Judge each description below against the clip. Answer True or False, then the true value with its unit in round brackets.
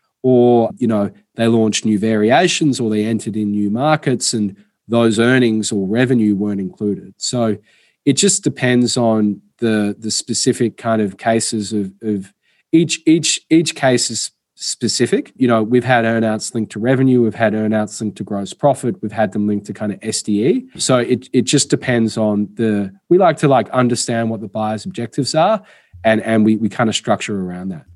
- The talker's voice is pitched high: False (115 Hz)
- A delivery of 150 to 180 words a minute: False (190 wpm)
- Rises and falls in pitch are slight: False (3.0 semitones)